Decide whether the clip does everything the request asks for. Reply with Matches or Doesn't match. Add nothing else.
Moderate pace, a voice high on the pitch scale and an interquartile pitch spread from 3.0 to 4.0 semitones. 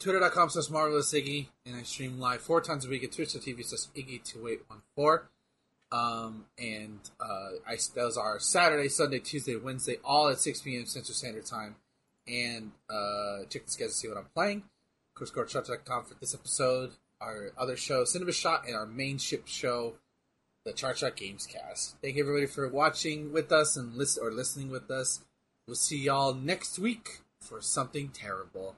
Doesn't match